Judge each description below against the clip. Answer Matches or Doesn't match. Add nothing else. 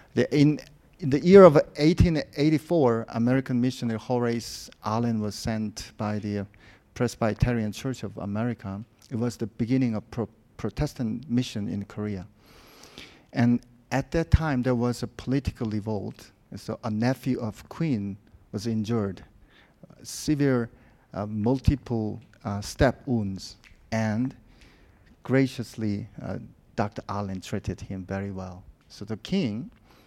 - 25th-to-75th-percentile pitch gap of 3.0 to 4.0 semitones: Matches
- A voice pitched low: Matches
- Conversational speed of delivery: Doesn't match